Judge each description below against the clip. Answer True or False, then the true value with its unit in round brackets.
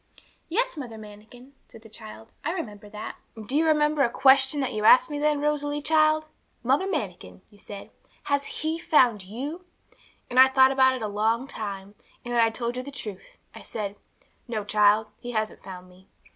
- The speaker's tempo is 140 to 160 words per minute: False (195 wpm)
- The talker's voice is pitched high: True (245 Hz)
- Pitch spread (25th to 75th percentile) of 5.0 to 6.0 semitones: True (5.6 semitones)